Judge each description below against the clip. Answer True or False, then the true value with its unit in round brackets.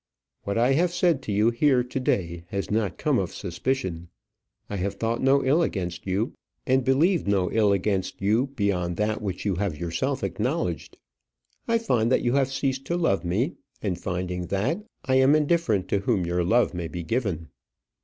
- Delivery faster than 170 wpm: True (185 wpm)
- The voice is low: True (105 Hz)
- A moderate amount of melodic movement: False (6.4 semitones)